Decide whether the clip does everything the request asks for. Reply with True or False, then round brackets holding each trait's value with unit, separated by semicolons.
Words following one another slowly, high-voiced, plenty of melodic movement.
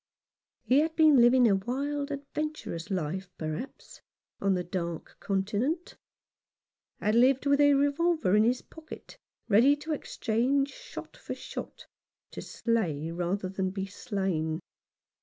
True (130 wpm; 235 Hz; 7.0 semitones)